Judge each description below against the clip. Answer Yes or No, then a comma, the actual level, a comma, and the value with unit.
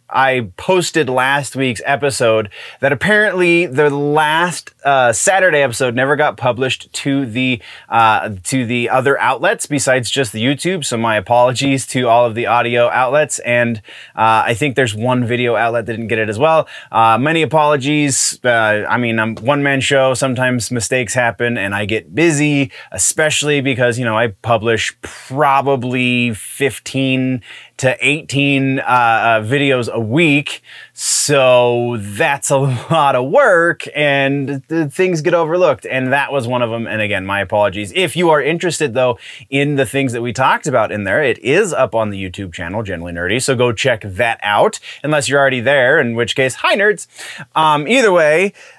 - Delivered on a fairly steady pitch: No, average, 3.4 semitones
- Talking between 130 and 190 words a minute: Yes, average, 175 wpm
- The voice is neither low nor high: No, low, 130 Hz